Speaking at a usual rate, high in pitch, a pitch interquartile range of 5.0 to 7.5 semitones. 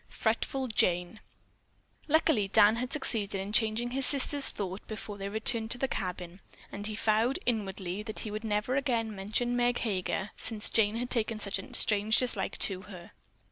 No: average, 175 wpm; high, 215 Hz; average, 3.2 semitones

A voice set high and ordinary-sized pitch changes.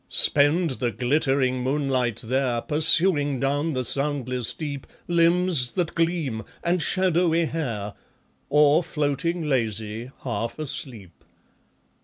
No: medium, 140 Hz; average, 4.5 semitones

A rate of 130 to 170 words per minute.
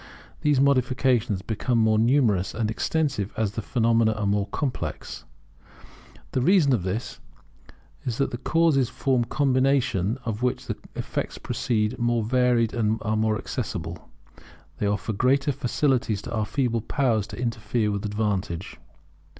Yes: average, 140 wpm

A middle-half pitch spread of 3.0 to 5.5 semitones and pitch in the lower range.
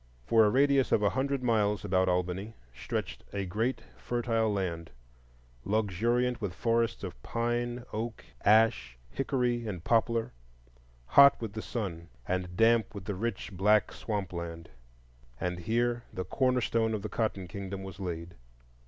Yes: average, 4.1 semitones; low, 105 Hz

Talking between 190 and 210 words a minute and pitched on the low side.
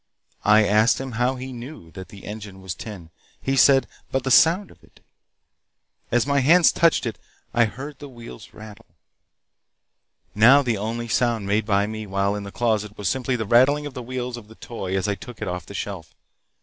Yes: average, 200 wpm; low, 115 Hz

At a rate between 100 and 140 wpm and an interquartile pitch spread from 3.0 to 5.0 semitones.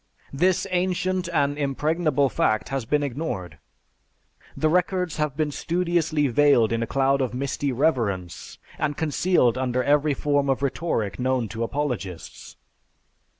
Yes: slow, 135 wpm; average, 4.0 semitones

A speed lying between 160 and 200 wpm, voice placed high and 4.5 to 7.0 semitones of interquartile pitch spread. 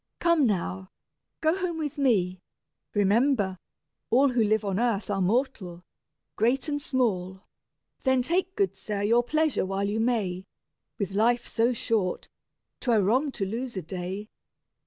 No: average, 145 wpm; high, 225 Hz; average, 5.2 semitones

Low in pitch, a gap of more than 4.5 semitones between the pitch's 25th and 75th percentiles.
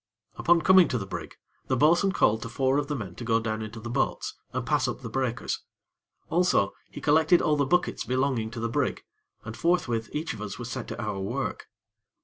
Yes: low, 130 Hz; average, 4.9 semitones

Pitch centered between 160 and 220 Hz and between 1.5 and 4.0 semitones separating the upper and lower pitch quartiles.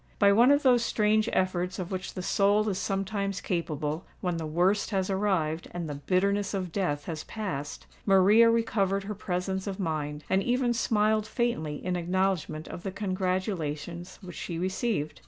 Yes: high, 190 Hz; average, 3.1 semitones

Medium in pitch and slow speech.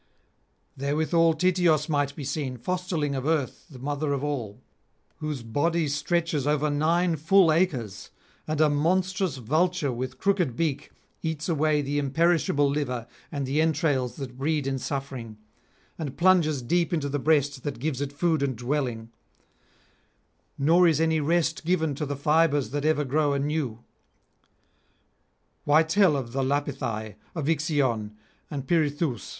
No: medium, 145 Hz; average, 145 wpm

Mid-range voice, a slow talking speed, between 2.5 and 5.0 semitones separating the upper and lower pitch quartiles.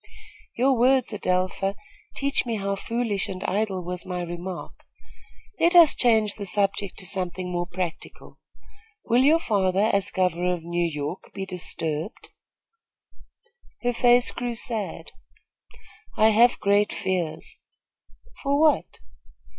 No: high, 200 Hz; slow, 125 wpm; average, 4.5 semitones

